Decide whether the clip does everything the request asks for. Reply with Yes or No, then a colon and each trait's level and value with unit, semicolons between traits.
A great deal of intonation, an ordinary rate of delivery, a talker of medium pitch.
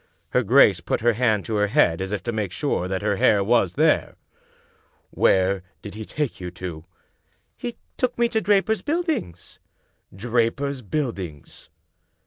No: wide, 6.8 semitones; average, 160 wpm; low, 110 Hz